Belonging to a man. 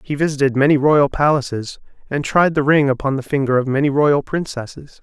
Yes: male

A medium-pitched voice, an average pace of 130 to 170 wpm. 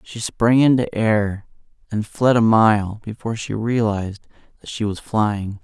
No: low, 110 Hz; average, 160 wpm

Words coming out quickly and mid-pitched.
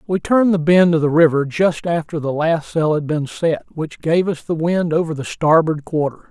Yes: fast, 230 wpm; medium, 160 Hz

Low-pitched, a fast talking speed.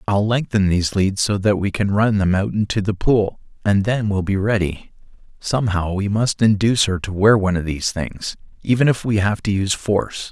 Yes: low, 100 Hz; fast, 215 wpm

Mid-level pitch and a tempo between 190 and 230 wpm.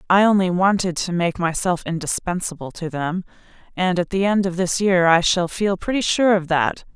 Yes: medium, 180 Hz; average, 200 wpm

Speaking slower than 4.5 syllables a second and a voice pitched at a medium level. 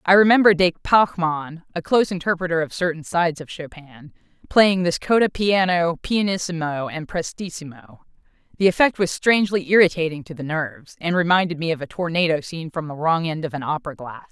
No: 5.6 syllables/s; medium, 170 Hz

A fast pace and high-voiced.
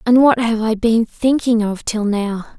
Yes: fast, 210 wpm; high, 225 Hz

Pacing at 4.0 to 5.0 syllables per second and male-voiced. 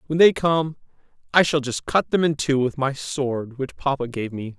Yes: 4.6 syllables/s; male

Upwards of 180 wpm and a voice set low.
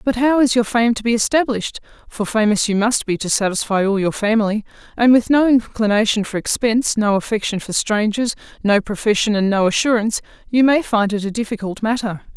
No: average, 195 wpm; high, 220 Hz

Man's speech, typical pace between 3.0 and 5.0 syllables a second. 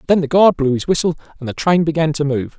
No: male; 6.5 syllables/s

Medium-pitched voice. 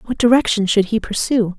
No: high, 220 Hz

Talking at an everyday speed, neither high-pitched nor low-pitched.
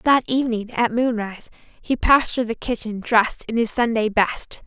No: average, 180 wpm; high, 230 Hz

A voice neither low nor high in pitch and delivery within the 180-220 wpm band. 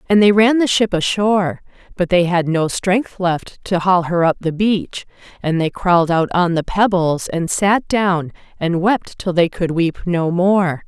Yes: medium, 180 Hz; average, 200 wpm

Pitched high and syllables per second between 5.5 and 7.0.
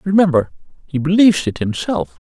No: medium, 160 Hz; 5.7 syllables/s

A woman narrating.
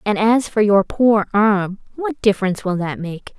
Yes: female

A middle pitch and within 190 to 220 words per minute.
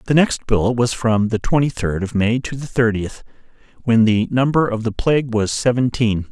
No: low, 120 Hz; average, 200 wpm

